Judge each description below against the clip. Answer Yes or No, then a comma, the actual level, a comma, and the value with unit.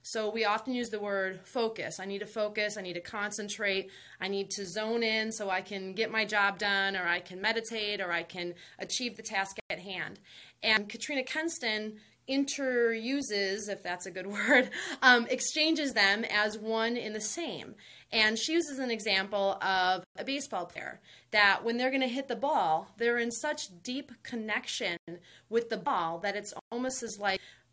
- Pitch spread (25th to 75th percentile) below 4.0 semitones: Yes, average, 3.5 semitones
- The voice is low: No, high, 215 Hz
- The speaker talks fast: No, average, 185 wpm